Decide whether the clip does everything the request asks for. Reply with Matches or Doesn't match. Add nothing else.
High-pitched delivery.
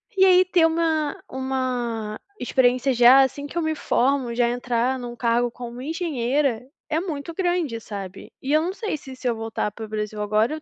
Matches